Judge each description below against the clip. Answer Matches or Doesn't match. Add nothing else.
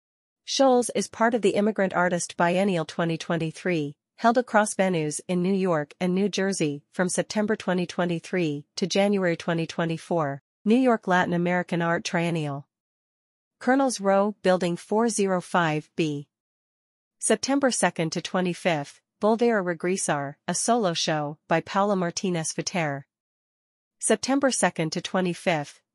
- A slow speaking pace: Matches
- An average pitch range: Matches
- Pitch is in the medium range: Matches